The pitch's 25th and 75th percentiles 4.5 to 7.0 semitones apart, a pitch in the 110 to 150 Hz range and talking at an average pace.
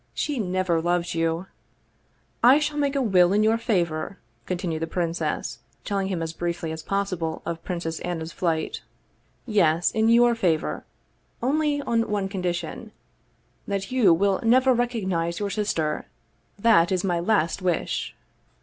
No: average, 4.9 semitones; medium, 185 Hz; average, 160 wpm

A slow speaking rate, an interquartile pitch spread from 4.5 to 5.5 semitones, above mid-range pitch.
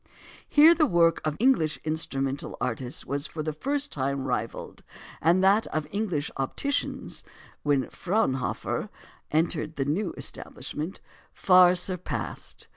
No: slow, 120 wpm; average, 5.1 semitones; medium, 160 Hz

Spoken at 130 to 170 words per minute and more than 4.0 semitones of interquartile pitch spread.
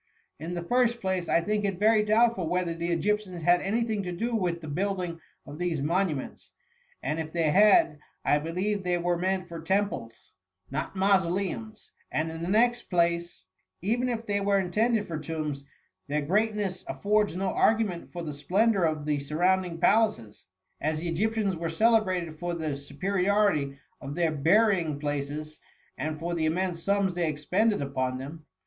No: average, 180 wpm; average, 4.4 semitones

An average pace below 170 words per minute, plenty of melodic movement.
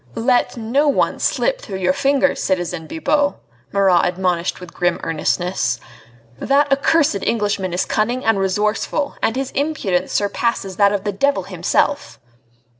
Yes: average, 140 wpm; wide, 6.9 semitones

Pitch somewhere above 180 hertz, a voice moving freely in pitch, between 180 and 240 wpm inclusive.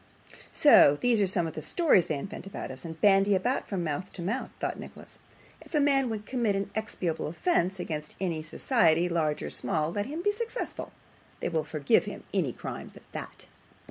Yes: high, 190 Hz; wide, 6.2 semitones; average, 195 wpm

